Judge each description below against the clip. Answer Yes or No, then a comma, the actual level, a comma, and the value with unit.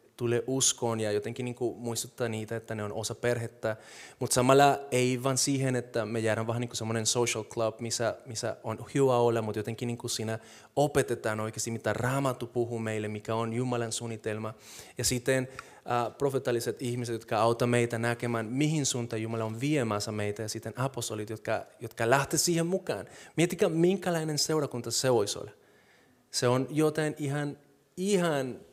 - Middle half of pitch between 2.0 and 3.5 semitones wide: Yes, average, 3.1 semitones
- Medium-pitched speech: No, low, 120 Hz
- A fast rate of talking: Yes, fast, 165 wpm